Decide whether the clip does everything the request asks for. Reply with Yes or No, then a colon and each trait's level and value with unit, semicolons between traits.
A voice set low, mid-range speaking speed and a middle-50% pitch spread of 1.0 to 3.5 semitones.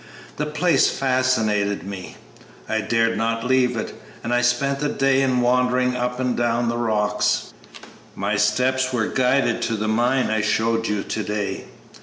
Yes: low, 120 Hz; average, 165 wpm; average, 2.8 semitones